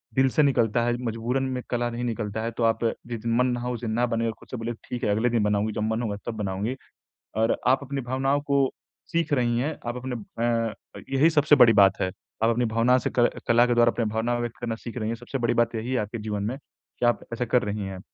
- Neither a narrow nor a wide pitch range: No, narrow, 1.8 semitones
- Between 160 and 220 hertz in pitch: No, low, 120 Hz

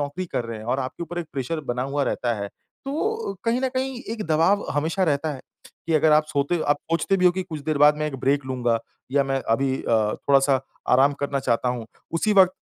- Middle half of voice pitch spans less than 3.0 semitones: No, average, 5.0 semitones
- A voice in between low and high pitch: Yes, medium, 145 Hz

